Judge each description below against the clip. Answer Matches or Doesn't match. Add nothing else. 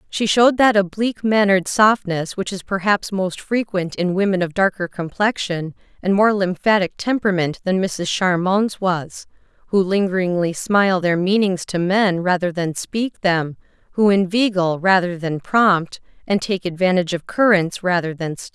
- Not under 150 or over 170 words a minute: Matches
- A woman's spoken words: Matches